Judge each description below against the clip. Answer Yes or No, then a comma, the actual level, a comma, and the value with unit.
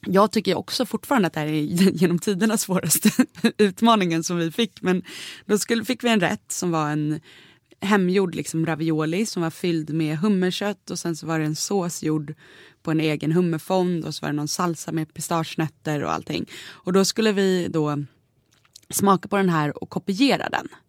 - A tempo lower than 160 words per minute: No, average, 190 wpm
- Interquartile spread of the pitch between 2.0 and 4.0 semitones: No, average, 4.5 semitones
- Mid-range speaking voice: Yes, medium, 175 Hz